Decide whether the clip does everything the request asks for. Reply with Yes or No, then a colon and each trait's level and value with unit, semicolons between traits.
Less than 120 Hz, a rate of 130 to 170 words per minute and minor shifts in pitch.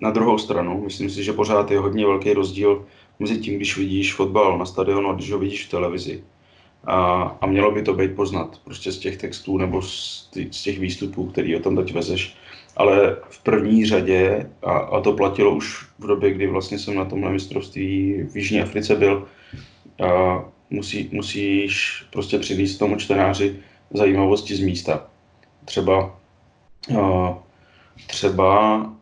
Yes: low, 100 Hz; average, 160 wpm; narrow, 1.1 semitones